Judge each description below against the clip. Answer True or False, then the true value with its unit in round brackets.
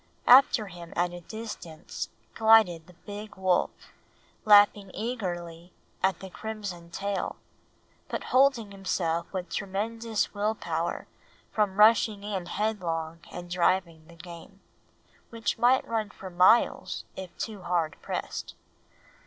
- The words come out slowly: True (120 wpm)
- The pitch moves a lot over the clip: False (3.8 semitones)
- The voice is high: True (195 Hz)